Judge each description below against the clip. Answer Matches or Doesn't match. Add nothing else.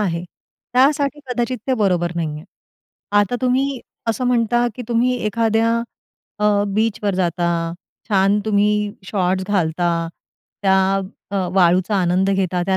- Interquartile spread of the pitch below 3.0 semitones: Doesn't match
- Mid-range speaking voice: Doesn't match